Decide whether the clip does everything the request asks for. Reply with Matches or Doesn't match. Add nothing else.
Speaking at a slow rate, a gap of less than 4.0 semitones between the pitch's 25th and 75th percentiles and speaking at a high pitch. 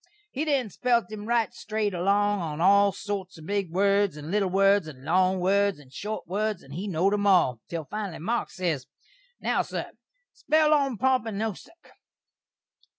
Doesn't match